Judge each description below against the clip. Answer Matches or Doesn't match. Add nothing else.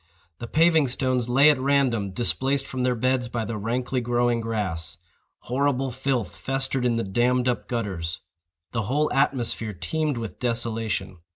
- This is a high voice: Doesn't match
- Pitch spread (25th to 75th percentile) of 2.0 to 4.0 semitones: Matches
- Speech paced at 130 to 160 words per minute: Matches